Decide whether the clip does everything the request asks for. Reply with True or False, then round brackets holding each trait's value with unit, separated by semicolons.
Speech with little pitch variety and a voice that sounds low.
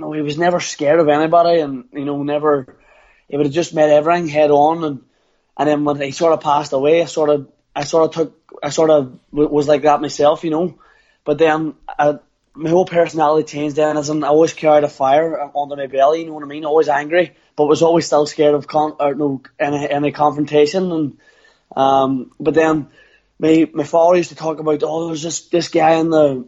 False (1.7 semitones; 150 Hz)